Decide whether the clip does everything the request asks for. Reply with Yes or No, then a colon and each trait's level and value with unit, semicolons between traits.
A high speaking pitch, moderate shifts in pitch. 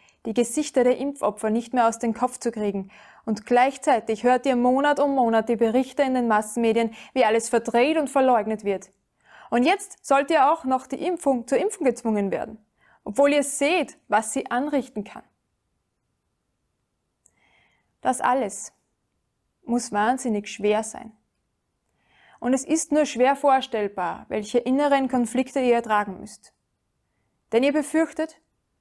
Yes: very high, 250 Hz; average, 3.8 semitones